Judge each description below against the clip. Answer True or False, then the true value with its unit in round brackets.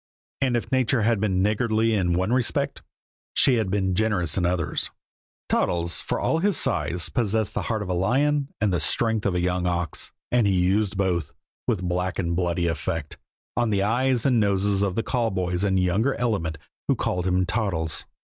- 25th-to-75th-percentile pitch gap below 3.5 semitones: False (4.1 semitones)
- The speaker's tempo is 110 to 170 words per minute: False (190 wpm)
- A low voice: True (100 Hz)